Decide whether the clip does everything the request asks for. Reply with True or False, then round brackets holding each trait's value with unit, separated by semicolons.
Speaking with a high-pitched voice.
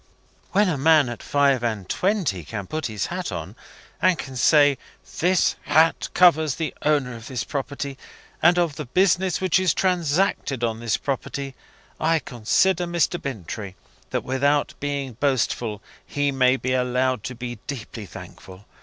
False (140 Hz)